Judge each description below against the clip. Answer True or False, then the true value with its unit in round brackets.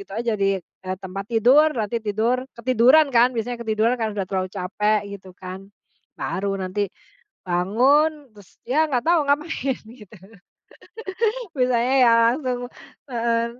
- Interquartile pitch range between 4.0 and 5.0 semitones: True (4.3 semitones)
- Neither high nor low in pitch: False (230 Hz)